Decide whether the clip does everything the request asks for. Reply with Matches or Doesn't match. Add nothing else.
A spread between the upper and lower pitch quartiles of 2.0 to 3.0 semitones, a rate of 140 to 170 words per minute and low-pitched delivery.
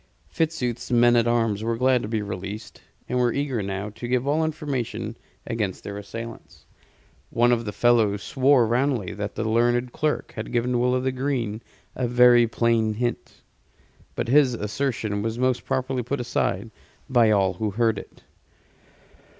Matches